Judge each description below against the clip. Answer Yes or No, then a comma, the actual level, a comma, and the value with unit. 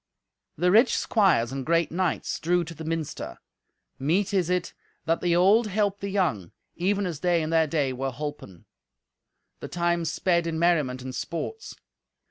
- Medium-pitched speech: Yes, medium, 170 Hz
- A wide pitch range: No, average, 3.2 semitones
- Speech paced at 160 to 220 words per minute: Yes, average, 165 wpm